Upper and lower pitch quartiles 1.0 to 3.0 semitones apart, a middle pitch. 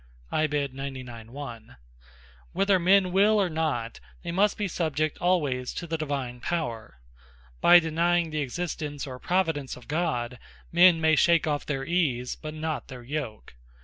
No: average, 4.8 semitones; medium, 155 Hz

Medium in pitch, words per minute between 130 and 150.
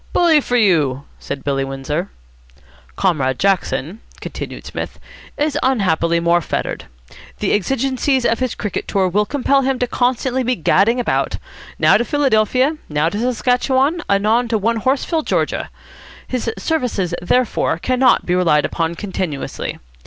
No: high, 220 Hz; average, 140 wpm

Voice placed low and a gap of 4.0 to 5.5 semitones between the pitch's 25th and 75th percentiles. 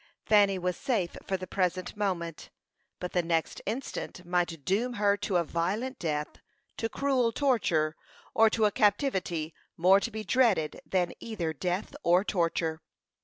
No: medium, 185 Hz; average, 4.3 semitones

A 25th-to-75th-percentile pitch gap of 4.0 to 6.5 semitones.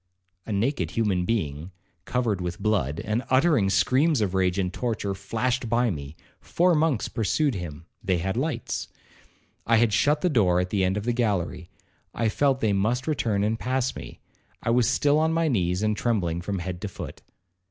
Yes: average, 5.2 semitones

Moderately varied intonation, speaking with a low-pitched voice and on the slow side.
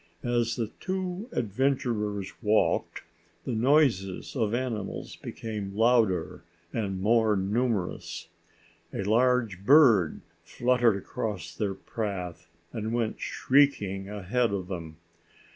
Yes: average, 3.9 semitones; low, 110 Hz; slow, 105 wpm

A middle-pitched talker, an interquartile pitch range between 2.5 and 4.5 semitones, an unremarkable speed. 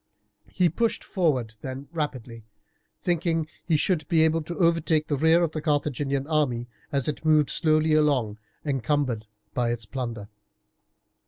Yes: medium, 150 Hz; average, 3.9 semitones; average, 150 wpm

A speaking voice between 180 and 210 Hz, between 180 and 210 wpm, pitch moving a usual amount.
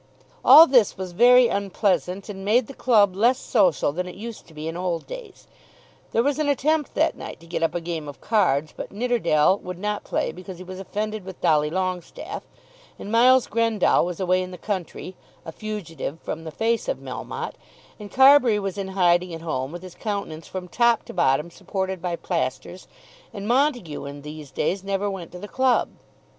Yes: high, 190 Hz; average, 195 wpm; average, 4.8 semitones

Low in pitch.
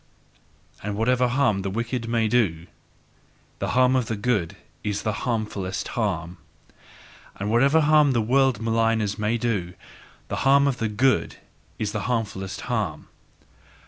Yes: low, 115 Hz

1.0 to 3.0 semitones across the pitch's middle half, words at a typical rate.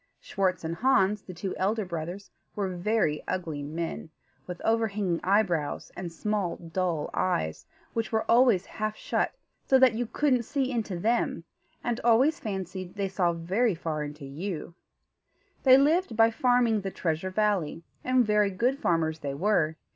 No: average, 5.0 semitones; average, 155 wpm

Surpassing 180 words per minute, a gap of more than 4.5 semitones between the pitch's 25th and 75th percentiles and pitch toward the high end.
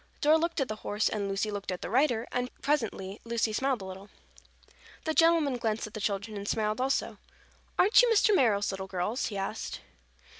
Yes: average, 195 wpm; average, 5.3 semitones; high, 220 Hz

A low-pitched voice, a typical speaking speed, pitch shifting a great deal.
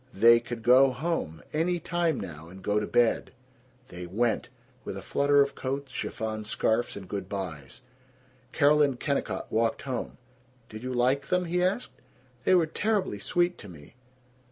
Yes: low, 125 Hz; average, 165 wpm; wide, 6.6 semitones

